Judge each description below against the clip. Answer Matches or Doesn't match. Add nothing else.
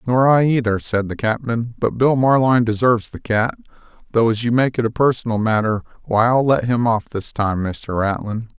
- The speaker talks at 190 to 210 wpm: Matches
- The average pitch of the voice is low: Matches